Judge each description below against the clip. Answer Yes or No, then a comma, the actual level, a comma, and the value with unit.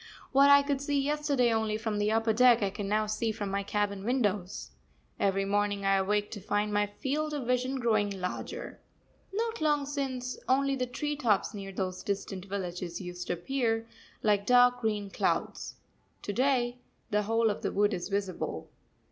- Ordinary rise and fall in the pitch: Yes, average, 4.1 semitones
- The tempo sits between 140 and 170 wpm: No, average, 180 wpm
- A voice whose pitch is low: No, high, 215 Hz